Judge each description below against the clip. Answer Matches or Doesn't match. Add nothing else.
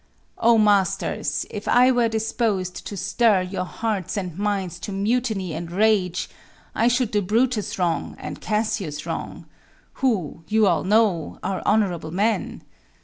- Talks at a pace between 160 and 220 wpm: Doesn't match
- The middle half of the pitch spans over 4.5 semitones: Doesn't match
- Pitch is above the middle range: Matches